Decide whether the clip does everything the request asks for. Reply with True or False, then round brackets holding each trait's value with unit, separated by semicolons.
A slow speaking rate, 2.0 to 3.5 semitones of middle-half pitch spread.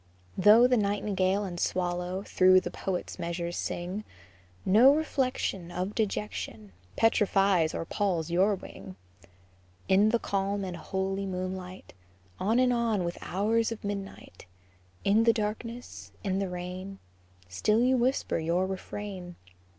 True (130 wpm; 2.9 semitones)